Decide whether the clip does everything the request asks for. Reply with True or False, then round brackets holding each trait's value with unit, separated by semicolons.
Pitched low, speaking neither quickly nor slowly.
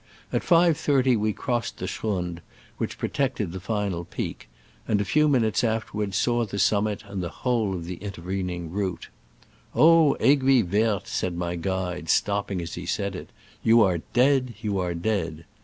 True (100 Hz; 175 wpm)